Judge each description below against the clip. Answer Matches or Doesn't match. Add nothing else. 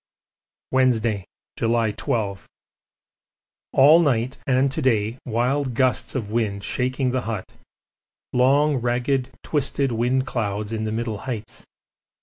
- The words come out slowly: Matches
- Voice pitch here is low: Matches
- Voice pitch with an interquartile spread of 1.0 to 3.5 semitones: Matches